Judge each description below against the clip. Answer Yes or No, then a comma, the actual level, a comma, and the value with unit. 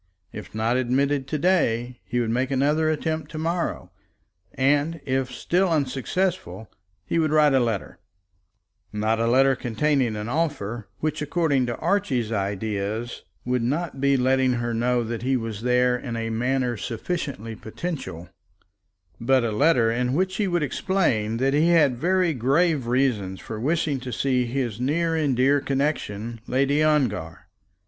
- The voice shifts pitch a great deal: No, average, 4.5 semitones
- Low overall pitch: Yes, low, 130 Hz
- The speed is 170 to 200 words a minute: No, average, 155 wpm